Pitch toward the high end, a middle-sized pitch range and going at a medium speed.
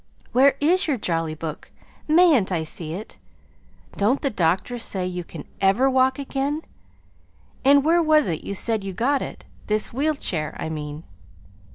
No: high, 225 Hz; wide, 8.4 semitones; average, 165 wpm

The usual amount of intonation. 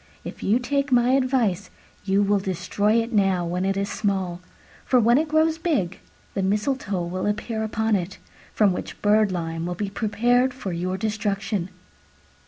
Yes: average, 4.1 semitones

